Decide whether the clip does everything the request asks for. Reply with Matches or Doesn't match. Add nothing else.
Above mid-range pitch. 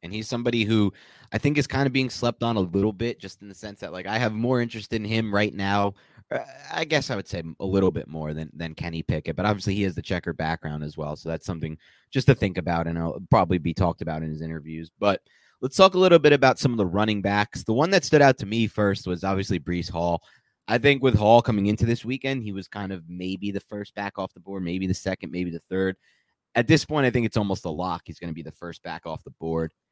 Doesn't match